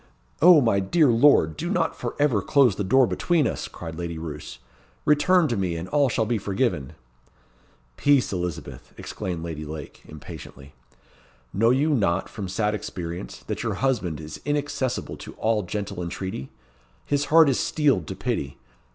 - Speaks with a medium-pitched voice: No, low, 105 Hz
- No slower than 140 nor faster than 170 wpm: Yes, average, 160 wpm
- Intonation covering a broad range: Yes, wide, 8.4 semitones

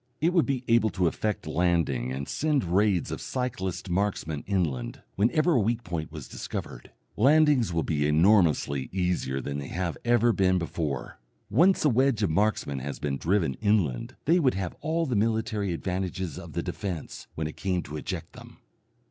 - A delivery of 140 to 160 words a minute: No, average, 175 wpm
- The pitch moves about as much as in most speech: No, wide, 6.5 semitones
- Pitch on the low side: Yes, very low, 95 Hz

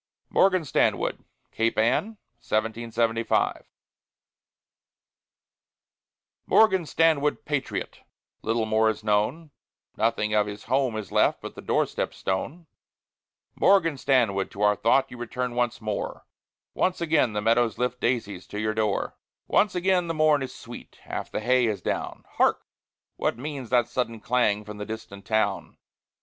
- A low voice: Yes, low, 115 Hz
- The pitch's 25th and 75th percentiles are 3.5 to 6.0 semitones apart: Yes, average, 4.4 semitones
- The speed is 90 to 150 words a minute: Yes, average, 140 wpm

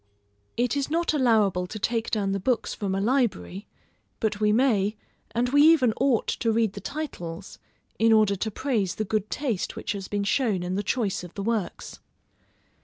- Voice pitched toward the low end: No, high, 220 Hz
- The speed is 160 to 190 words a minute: Yes, average, 185 wpm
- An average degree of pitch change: Yes, average, 3.9 semitones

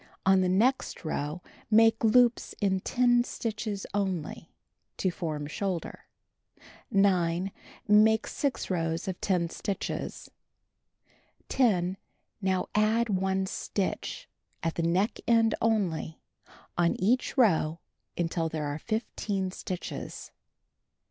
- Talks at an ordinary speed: No, slow, 110 wpm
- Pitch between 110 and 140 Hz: No, high, 190 Hz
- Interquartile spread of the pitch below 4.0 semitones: No, average, 4.3 semitones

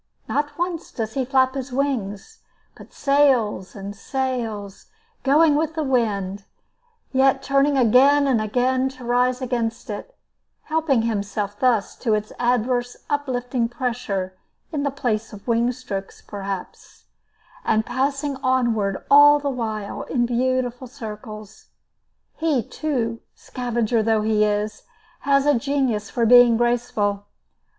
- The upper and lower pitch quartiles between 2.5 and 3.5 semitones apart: No, average, 3.9 semitones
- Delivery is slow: Yes, slow, 130 wpm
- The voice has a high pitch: Yes, high, 245 Hz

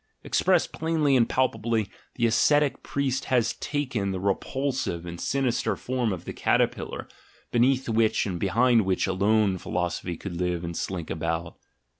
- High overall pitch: No, low, 110 Hz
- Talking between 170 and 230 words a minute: No, average, 145 wpm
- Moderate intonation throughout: No, wide, 6.0 semitones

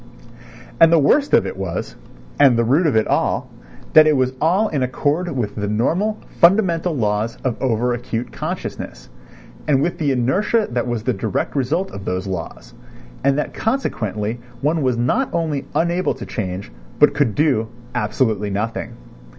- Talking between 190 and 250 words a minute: No, average, 165 wpm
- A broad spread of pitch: Yes, wide, 6.5 semitones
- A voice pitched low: Yes, low, 130 Hz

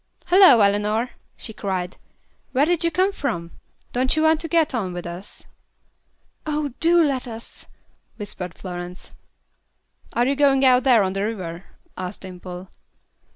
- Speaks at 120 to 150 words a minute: Yes, average, 145 wpm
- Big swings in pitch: Yes, wide, 7.8 semitones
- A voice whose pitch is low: No, high, 230 Hz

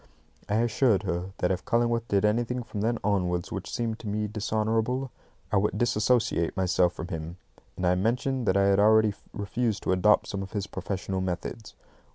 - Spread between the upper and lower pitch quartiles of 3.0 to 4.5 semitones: Yes, average, 3.5 semitones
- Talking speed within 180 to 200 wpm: Yes, average, 185 wpm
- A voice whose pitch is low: Yes, low, 105 Hz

